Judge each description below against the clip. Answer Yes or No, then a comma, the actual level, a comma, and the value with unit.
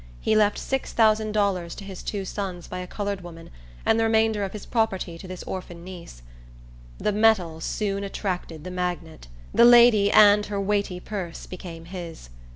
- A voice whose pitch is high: Yes, high, 195 Hz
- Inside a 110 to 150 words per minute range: No, average, 175 wpm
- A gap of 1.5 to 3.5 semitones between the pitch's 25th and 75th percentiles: Yes, average, 3.0 semitones